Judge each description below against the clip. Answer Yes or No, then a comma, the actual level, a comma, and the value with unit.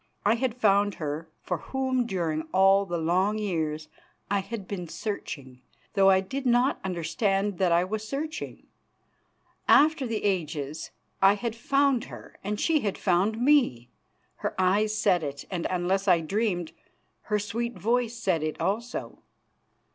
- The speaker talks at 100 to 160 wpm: Yes, average, 150 wpm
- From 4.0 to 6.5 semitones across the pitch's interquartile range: Yes, average, 4.9 semitones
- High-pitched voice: Yes, high, 195 Hz